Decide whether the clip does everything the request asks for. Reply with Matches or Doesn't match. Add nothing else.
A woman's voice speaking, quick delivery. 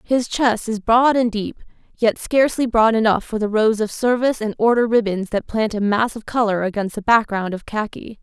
Matches